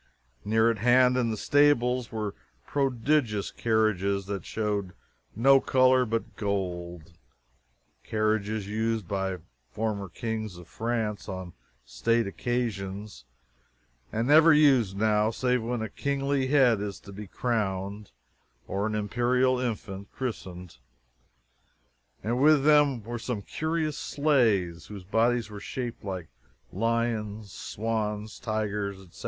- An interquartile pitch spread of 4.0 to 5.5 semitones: No, average, 3.6 semitones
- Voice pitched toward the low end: Yes, low, 110 Hz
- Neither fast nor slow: No, slow, 120 wpm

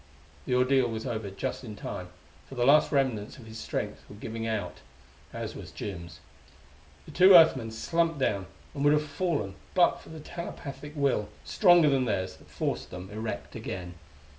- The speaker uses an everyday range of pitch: No, wide, 6.0 semitones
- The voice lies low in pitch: Yes, low, 125 Hz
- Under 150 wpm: No, average, 180 wpm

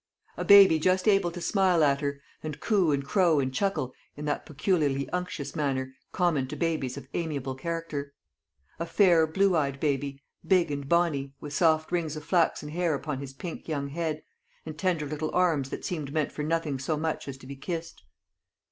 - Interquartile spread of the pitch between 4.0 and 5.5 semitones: No, average, 3.5 semitones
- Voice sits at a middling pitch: Yes, medium, 155 Hz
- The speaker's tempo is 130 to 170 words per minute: No, average, 190 wpm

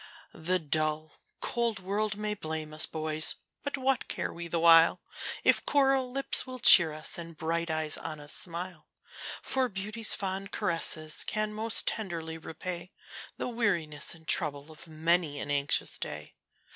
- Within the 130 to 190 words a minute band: Yes, average, 155 wpm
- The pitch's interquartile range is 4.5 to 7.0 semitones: Yes, average, 5.2 semitones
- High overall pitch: No, medium, 170 Hz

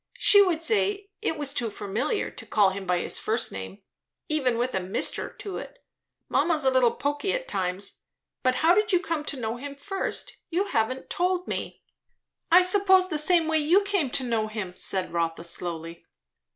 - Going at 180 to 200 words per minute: Yes, average, 190 wpm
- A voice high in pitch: Yes, very high, 280 Hz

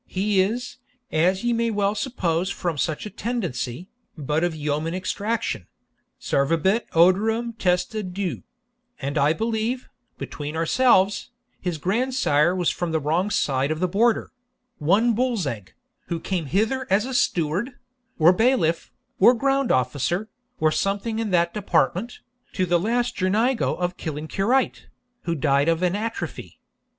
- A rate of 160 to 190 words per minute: No, average, 140 wpm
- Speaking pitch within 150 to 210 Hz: Yes, medium, 185 Hz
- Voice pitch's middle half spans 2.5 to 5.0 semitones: No, wide, 5.6 semitones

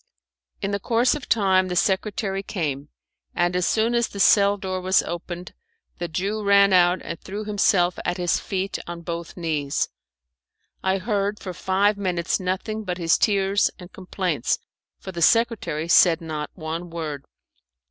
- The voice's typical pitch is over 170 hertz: Yes, medium, 185 Hz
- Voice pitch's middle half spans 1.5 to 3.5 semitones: Yes, average, 2.7 semitones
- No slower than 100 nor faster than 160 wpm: Yes, average, 155 wpm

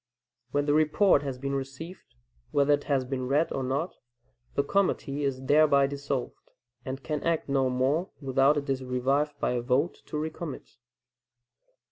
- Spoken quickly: No, average, 160 wpm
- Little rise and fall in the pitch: Yes, narrow, 2.1 semitones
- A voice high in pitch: No, medium, 140 Hz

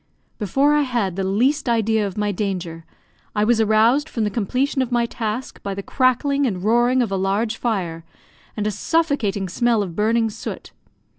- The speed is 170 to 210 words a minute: Yes, average, 180 wpm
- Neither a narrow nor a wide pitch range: Yes, average, 3.9 semitones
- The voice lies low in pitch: No, high, 220 Hz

